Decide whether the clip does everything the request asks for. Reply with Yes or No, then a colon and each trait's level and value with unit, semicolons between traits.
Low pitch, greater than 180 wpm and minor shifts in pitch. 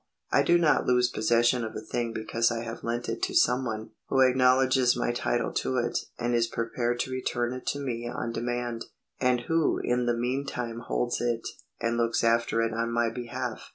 Yes: low, 120 Hz; average, 200 wpm; narrow, 1.3 semitones